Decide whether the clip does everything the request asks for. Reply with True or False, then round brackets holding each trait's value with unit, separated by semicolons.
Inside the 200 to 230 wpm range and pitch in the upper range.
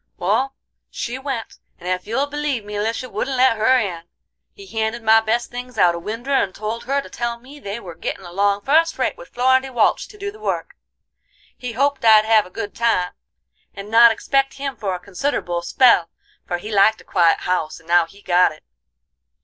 True (205 wpm; 225 Hz)